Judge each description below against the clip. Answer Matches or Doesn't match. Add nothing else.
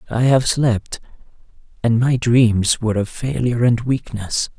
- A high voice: Doesn't match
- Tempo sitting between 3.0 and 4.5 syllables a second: Matches